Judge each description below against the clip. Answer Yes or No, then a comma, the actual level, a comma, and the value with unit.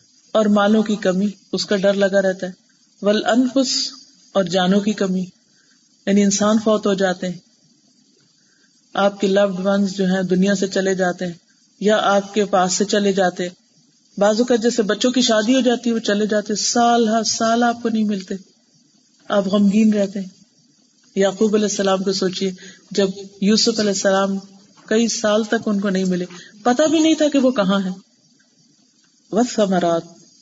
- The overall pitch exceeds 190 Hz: Yes, high, 205 Hz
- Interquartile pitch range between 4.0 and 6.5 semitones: No, average, 3.0 semitones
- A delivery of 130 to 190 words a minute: Yes, average, 175 wpm